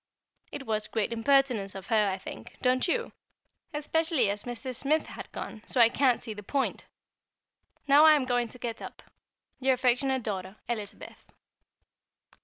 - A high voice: Yes, high, 245 Hz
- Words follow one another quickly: No, average, 160 wpm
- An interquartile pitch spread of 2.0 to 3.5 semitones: No, average, 4.0 semitones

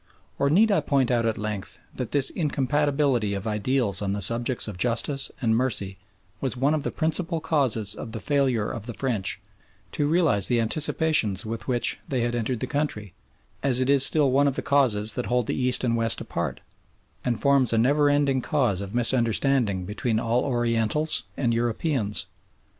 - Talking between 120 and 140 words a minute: No, average, 185 wpm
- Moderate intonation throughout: Yes, average, 4.0 semitones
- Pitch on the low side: Yes, low, 125 Hz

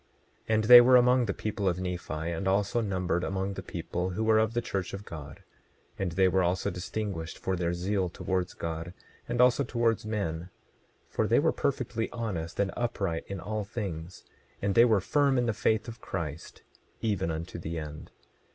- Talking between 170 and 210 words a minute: Yes, average, 190 wpm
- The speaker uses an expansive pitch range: No, average, 4.1 semitones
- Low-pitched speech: Yes, very low, 95 Hz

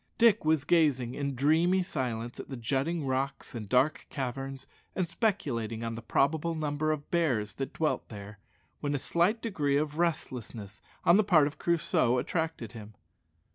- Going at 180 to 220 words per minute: No, average, 165 wpm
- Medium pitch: Yes, medium, 145 Hz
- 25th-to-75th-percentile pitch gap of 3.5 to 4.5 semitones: No, average, 4.9 semitones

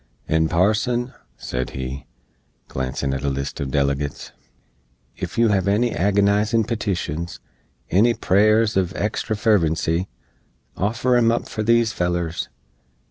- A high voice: No, low, 100 Hz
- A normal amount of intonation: No, wide, 5.8 semitones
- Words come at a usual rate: No, slow, 125 wpm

